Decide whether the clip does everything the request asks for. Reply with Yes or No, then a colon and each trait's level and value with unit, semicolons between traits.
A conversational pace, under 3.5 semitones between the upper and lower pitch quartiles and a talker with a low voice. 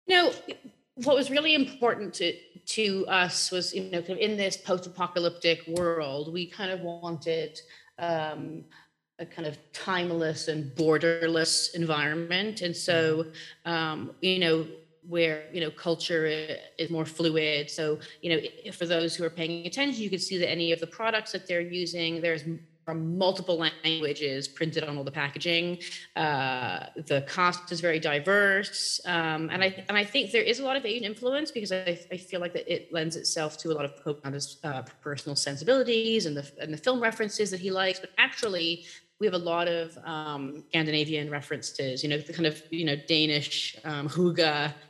No: average, 180 wpm; average, 3.0 semitones; medium, 165 Hz